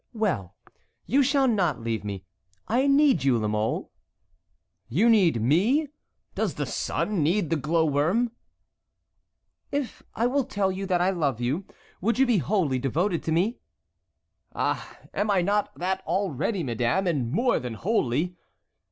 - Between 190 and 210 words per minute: No, average, 150 wpm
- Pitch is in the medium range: Yes, medium, 180 Hz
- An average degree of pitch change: No, wide, 8.0 semitones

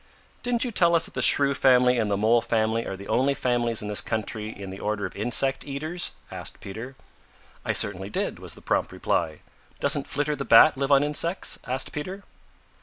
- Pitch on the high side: No, low, 125 Hz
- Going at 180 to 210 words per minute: Yes, average, 200 wpm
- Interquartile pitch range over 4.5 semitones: Yes, average, 5.3 semitones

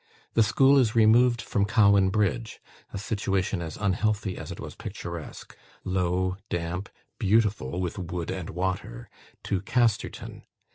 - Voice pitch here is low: Yes, low, 100 Hz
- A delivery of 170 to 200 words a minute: No, slow, 135 wpm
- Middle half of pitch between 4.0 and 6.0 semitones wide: No, average, 3.2 semitones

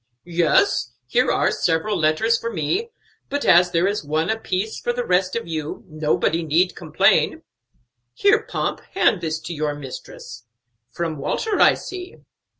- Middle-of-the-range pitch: Yes, medium, 175 Hz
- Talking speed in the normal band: Yes, average, 150 wpm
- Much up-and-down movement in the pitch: Yes, wide, 6.0 semitones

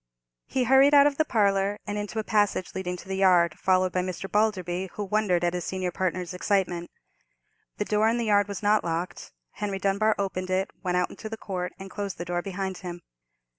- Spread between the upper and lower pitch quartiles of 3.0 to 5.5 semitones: No, narrow, 2.5 semitones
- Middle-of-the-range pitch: No, high, 195 Hz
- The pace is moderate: No, fast, 210 wpm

